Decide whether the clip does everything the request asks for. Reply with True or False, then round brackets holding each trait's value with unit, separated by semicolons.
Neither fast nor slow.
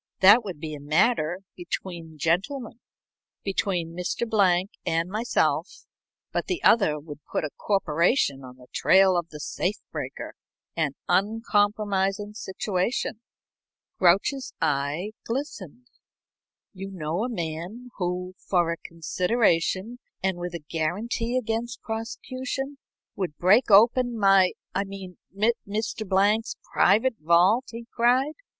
False (120 wpm)